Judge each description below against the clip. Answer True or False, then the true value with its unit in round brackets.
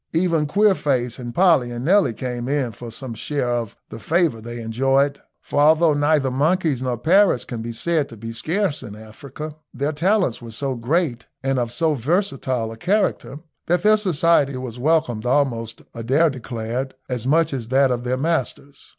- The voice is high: False (135 Hz)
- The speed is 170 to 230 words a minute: True (175 wpm)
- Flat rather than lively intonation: False (4.9 semitones)